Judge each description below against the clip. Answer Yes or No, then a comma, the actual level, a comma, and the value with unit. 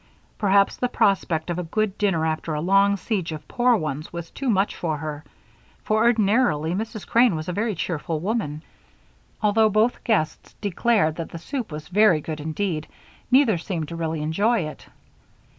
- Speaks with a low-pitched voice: No, medium, 185 Hz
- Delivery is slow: No, average, 175 wpm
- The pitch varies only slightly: No, average, 5.3 semitones